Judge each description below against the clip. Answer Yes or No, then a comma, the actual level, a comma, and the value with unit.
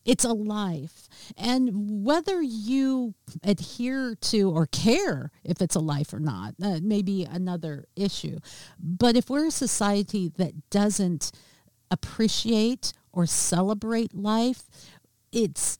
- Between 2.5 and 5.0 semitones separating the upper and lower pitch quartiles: No, wide, 5.6 semitones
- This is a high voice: Yes, high, 200 Hz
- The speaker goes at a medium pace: No, slow, 125 wpm